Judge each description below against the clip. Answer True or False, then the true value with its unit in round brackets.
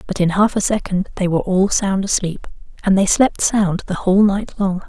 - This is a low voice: False (190 Hz)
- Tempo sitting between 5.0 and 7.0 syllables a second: True (5.3 syllables/s)